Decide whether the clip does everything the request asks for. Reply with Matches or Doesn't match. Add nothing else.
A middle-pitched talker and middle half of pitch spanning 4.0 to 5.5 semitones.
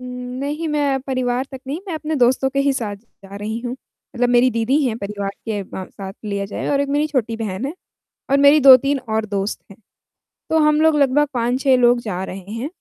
Doesn't match